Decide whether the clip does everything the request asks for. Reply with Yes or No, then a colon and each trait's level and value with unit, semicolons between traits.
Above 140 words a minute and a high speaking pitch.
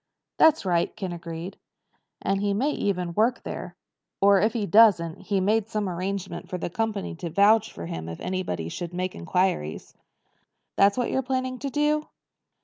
Yes: average, 170 wpm; high, 195 Hz